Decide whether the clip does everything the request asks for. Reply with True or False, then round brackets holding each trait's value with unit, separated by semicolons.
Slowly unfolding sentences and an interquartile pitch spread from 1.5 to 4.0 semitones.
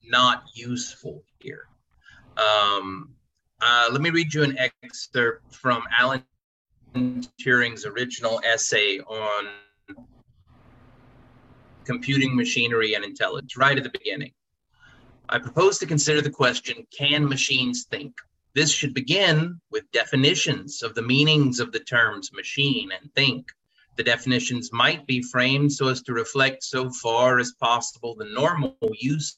True (130 wpm; 2.9 semitones)